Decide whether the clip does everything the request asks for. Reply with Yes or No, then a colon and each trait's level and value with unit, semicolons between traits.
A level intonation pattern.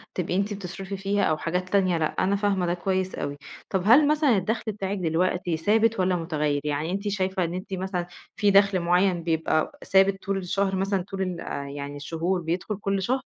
Yes: narrow, 2.3 semitones